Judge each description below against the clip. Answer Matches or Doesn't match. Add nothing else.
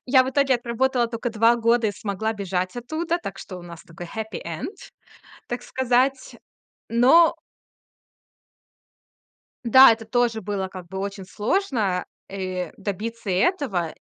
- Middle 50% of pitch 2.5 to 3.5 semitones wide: Doesn't match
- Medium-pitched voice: Doesn't match